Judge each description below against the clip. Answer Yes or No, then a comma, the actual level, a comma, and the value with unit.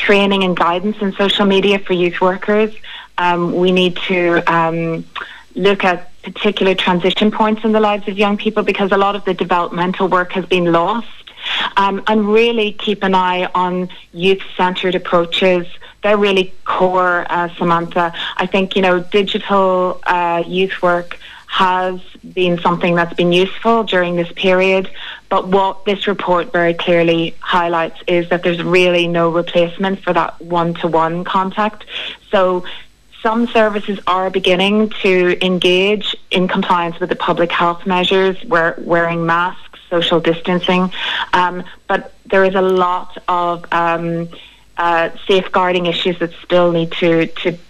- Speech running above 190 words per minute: No, average, 150 wpm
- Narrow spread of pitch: Yes, narrow, 2.0 semitones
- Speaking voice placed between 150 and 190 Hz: Yes, medium, 185 Hz